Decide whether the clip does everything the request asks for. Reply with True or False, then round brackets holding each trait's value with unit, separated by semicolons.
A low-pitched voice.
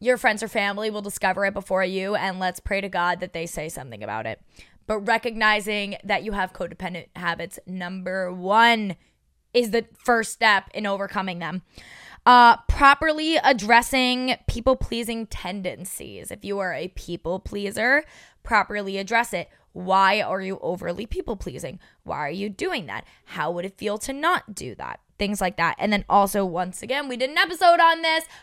False (200 Hz)